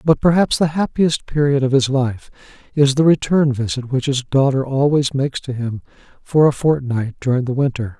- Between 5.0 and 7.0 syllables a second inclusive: Yes, 5.1 syllables/s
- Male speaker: Yes, male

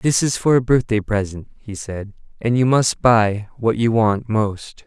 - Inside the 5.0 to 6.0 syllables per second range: No, 4.1 syllables/s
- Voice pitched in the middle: No, low, 110 Hz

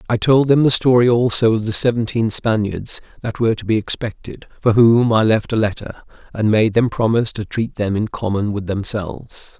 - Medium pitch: No, low, 110 Hz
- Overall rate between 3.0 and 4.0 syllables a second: No, 5.2 syllables/s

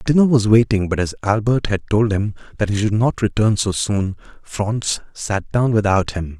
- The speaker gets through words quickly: No, average, 195 wpm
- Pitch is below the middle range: Yes, low, 105 Hz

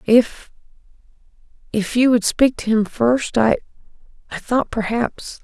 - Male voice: No, female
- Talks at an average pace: No, slow, 100 wpm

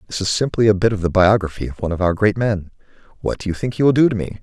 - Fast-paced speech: Yes, fast, 310 wpm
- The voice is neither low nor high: No, low, 100 Hz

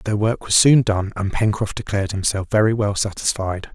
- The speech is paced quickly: No, average, 190 wpm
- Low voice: Yes, low, 105 Hz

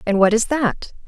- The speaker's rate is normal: No, fast, 225 wpm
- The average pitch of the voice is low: No, high, 225 Hz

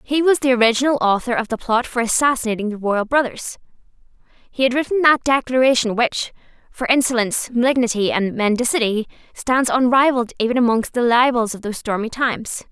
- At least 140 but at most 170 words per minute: Yes, average, 160 wpm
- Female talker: Yes, female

